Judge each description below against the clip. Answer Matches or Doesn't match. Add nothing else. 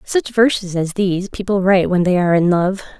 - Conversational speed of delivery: Doesn't match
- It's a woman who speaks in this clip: Matches